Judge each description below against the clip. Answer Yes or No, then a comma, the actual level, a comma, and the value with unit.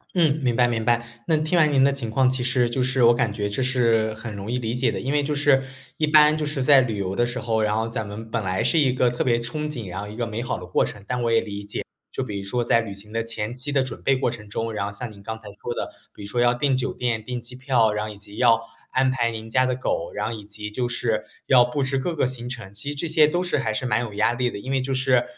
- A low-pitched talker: Yes, low, 120 Hz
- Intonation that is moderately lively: Yes, average, 3.2 semitones